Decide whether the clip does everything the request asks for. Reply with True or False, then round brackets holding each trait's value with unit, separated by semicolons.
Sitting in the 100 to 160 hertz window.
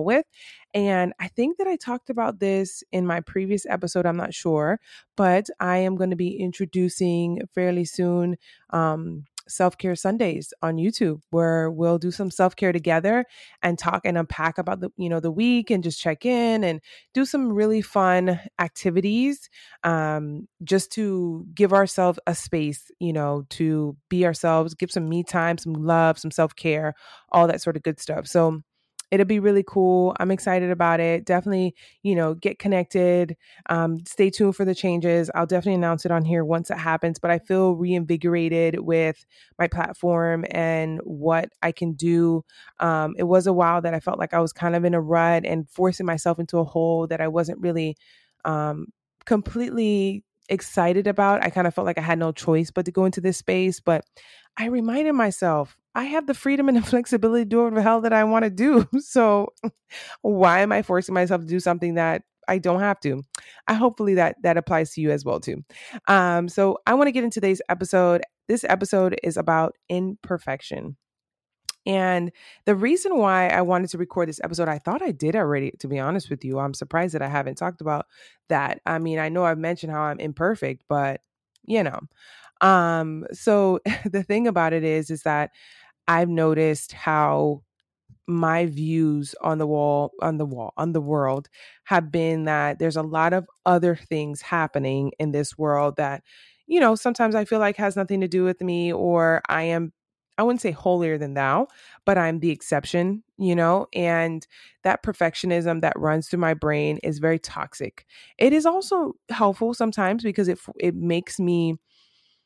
False (175 Hz)